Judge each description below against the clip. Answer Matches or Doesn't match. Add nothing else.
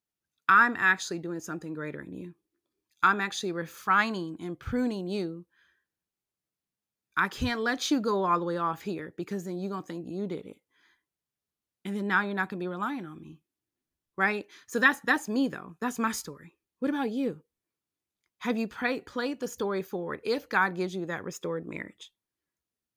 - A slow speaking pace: Doesn't match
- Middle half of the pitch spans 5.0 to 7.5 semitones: Matches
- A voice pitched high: Matches